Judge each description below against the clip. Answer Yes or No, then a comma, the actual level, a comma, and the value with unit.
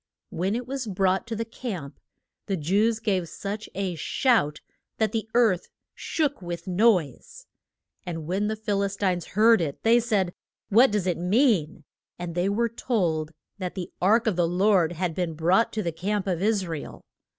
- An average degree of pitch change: Yes, average, 4.1 semitones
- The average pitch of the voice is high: Yes, high, 195 Hz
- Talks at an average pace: Yes, average, 185 wpm